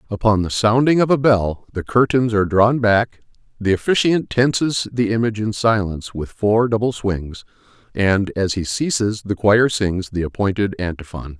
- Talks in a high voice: No, low, 105 Hz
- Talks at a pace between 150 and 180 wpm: Yes, average, 170 wpm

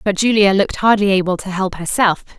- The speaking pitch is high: Yes, high, 195 Hz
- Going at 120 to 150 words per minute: No, average, 200 wpm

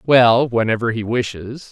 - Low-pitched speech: Yes, low, 120 Hz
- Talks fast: No, average, 140 wpm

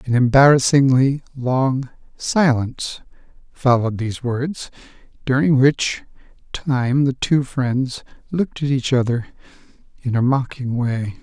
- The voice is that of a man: Yes, male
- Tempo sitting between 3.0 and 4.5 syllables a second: Yes, 4.2 syllables/s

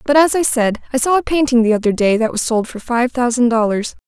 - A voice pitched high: Yes, high, 245 Hz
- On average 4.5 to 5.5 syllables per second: No, 5.9 syllables/s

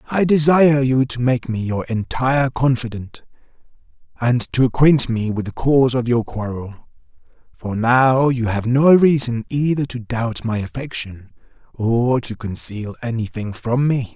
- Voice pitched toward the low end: Yes, low, 125 Hz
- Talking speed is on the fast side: No, average, 155 wpm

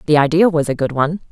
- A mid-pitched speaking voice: Yes, medium, 155 Hz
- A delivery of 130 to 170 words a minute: No, fast, 275 wpm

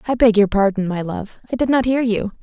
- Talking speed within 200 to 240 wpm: No, fast, 270 wpm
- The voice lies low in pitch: No, high, 220 Hz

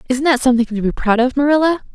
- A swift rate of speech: Yes, fast, 245 wpm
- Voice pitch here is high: Yes, very high, 260 Hz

